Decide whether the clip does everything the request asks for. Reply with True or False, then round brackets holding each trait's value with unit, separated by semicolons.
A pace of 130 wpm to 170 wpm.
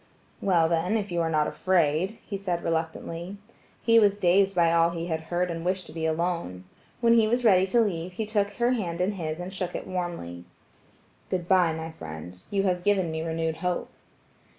False (200 wpm)